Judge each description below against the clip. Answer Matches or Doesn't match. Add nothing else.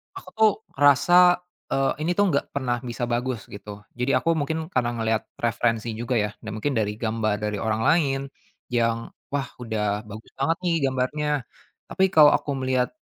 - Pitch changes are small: Doesn't match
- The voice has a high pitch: Doesn't match